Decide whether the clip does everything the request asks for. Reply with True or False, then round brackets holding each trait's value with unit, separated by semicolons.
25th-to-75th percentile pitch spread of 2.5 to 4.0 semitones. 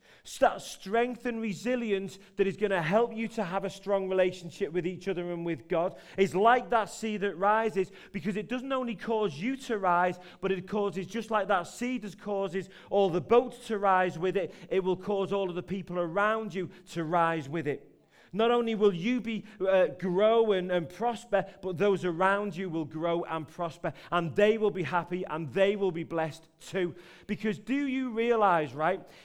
True (3.2 semitones)